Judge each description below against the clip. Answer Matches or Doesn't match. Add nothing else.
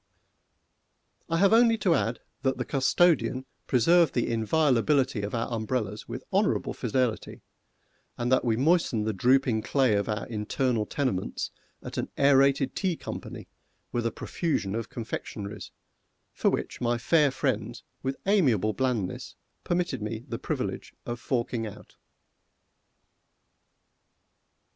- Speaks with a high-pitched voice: Doesn't match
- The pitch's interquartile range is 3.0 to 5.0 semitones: Matches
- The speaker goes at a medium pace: Doesn't match